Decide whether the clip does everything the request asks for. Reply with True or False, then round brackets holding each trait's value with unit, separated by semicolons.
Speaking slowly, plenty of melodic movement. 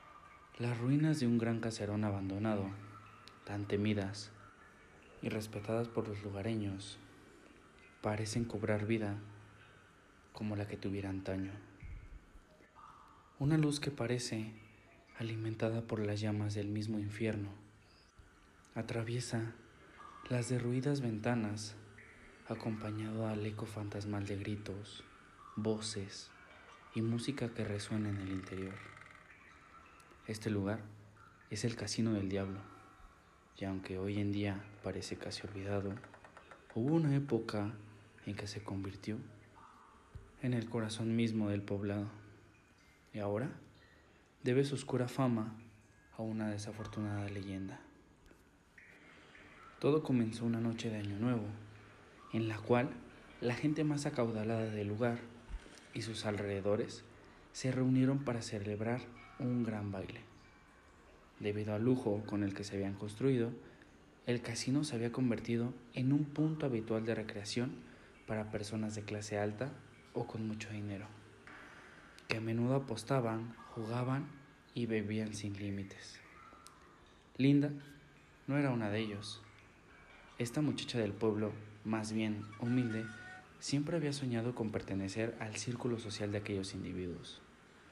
False (120 wpm; 2.6 semitones)